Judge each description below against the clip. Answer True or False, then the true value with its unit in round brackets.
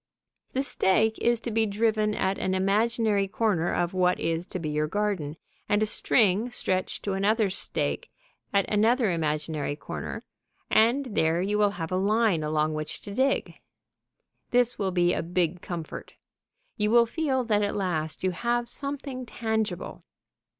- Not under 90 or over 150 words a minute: False (160 wpm)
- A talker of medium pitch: False (200 Hz)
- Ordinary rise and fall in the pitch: True (4.4 semitones)